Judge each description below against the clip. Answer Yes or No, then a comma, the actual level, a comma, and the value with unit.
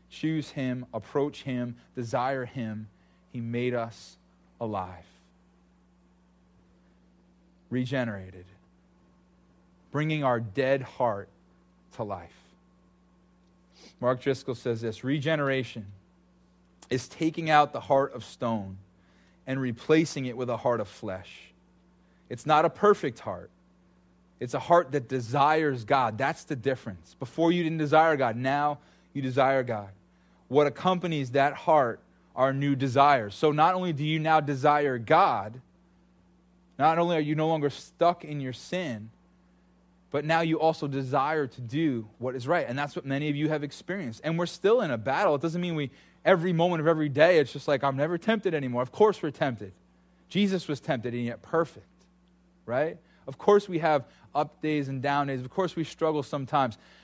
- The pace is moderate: Yes, average, 160 wpm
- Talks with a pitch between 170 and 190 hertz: No, medium, 140 Hz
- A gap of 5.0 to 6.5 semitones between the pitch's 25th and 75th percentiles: Yes, wide, 5.4 semitones